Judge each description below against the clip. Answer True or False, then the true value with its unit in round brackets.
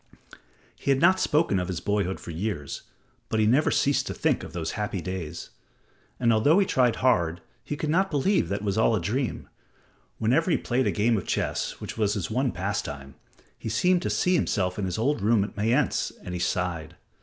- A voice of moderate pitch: False (110 Hz)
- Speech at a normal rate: False (210 wpm)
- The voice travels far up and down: True (6.9 semitones)